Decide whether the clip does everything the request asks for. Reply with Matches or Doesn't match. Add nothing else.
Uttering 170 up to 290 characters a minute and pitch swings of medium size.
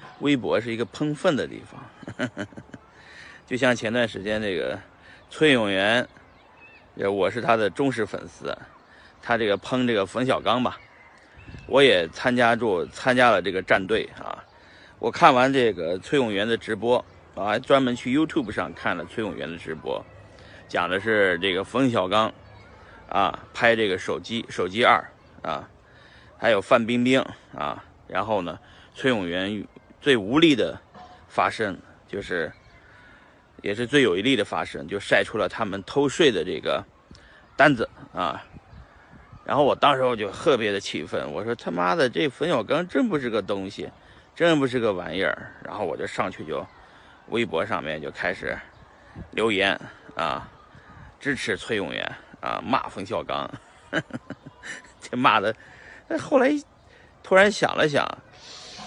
Doesn't match